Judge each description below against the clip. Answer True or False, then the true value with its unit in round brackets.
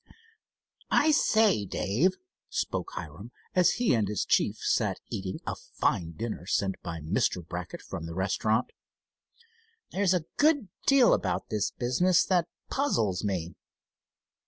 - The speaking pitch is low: True (110 Hz)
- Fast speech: False (135 wpm)